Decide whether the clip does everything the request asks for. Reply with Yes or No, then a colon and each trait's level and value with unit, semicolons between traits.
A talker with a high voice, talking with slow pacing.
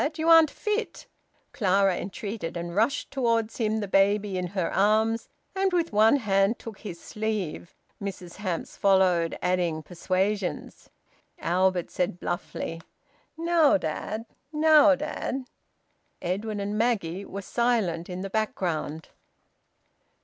Yes: high, 200 Hz; slow, 120 wpm